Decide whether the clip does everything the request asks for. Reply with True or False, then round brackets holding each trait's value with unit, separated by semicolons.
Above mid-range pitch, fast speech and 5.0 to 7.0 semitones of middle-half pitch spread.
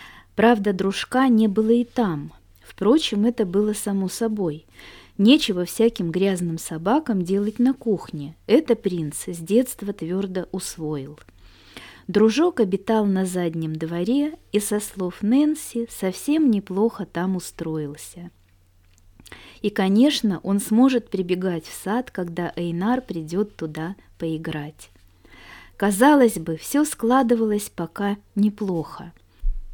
False (195 Hz; 110 wpm; 5.3 semitones)